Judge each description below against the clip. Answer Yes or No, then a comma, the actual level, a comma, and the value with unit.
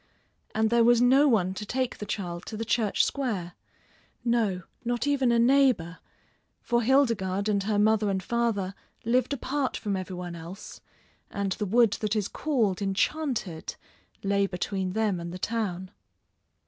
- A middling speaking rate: Yes, average, 160 wpm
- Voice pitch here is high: Yes, high, 215 Hz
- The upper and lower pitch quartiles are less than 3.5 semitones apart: No, average, 4.0 semitones